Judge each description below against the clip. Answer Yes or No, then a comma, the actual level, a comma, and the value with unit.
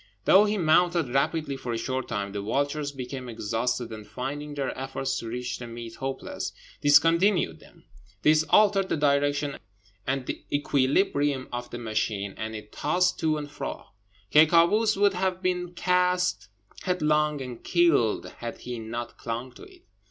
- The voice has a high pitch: No, medium, 140 Hz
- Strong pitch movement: Yes, wide, 5.8 semitones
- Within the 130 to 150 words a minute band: No, average, 160 wpm